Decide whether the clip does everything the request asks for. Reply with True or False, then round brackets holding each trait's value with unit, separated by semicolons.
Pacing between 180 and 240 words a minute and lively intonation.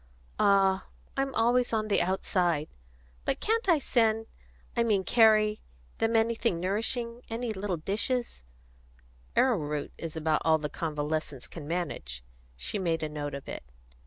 False (145 wpm; 6.7 semitones)